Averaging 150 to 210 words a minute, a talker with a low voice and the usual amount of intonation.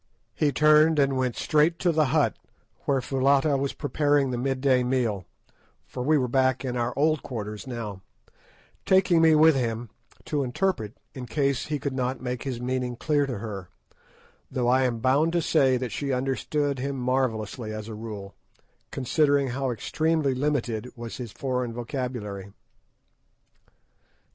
Yes: average, 160 wpm; low, 130 Hz; average, 3.1 semitones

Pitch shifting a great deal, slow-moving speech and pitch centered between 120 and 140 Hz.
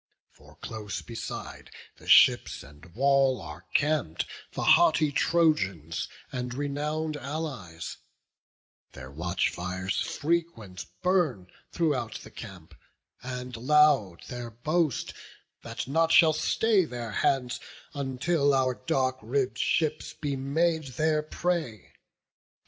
Yes: wide, 6.1 semitones; slow, 110 wpm; low, 135 Hz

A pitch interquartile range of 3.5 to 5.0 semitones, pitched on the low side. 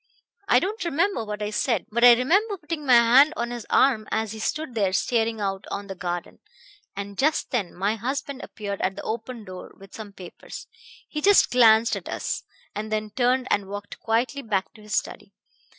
No: average, 4.2 semitones; high, 225 Hz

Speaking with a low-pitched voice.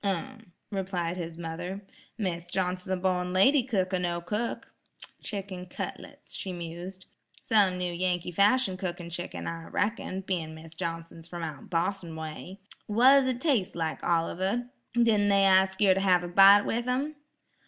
No: medium, 185 Hz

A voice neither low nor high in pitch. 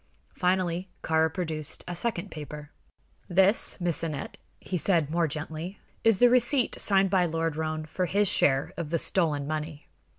Yes: medium, 170 Hz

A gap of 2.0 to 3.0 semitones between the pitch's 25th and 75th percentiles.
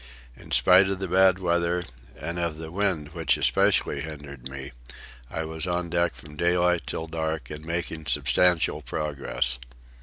Yes: narrow, 2.6 semitones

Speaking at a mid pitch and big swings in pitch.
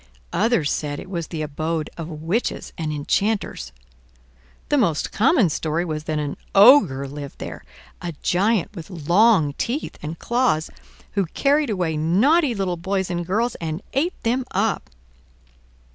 Yes: medium, 175 Hz; wide, 6.1 semitones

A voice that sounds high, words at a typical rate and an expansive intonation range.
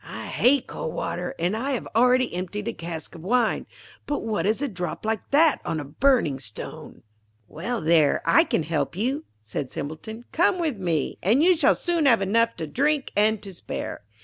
Yes: high, 215 Hz; average, 195 wpm; wide, 7.4 semitones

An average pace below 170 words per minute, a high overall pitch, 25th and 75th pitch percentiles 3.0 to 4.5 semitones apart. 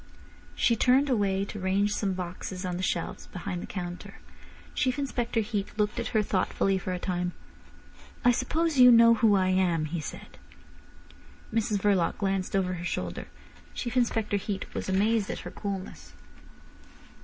Yes: average, 160 wpm; high, 200 Hz; average, 3.7 semitones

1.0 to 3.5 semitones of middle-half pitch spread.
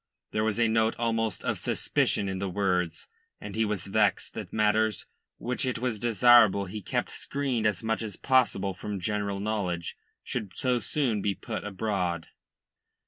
Yes: narrow, 2.6 semitones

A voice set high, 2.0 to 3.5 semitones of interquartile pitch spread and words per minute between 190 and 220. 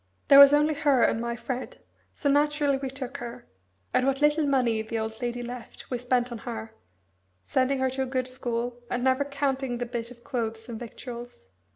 Yes: very high, 250 Hz; narrow, 2.5 semitones; average, 200 wpm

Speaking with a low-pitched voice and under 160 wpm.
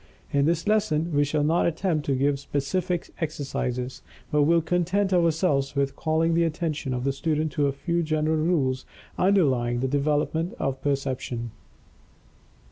No: medium, 150 Hz; average, 150 wpm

